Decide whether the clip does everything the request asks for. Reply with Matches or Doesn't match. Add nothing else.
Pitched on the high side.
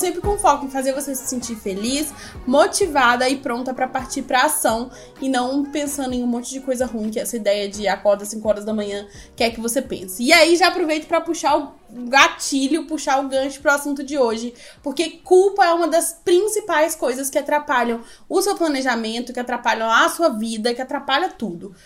Matches